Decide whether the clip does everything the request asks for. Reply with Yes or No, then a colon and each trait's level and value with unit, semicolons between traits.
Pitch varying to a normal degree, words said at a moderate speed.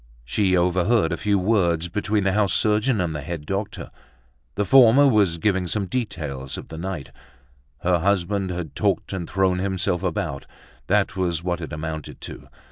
Yes: average, 3.5 semitones; average, 170 wpm